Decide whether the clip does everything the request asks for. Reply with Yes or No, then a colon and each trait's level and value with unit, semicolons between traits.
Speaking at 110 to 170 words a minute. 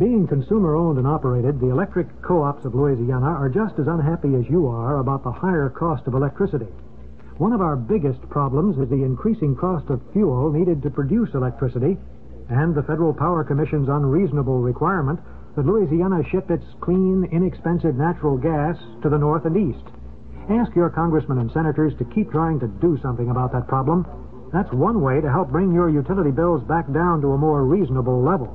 No: average, 185 wpm